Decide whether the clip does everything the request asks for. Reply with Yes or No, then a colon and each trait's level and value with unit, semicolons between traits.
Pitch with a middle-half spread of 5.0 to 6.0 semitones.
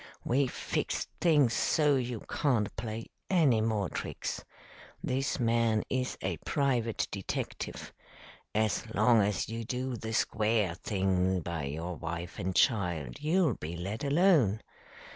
Yes: average, 5.3 semitones